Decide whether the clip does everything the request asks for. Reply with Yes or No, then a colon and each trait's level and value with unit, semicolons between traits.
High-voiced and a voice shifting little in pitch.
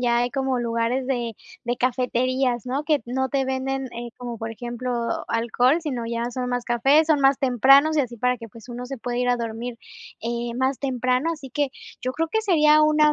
Yes: very high, 250 Hz; narrow, 2.2 semitones